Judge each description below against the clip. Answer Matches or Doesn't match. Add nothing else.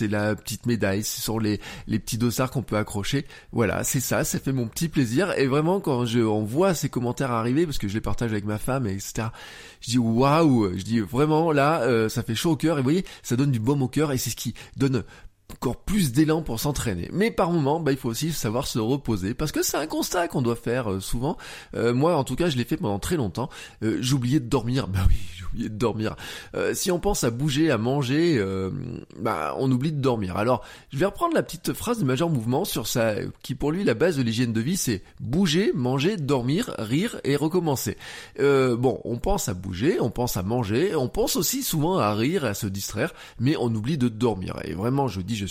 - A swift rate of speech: Matches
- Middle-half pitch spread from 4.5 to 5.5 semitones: Matches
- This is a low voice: Matches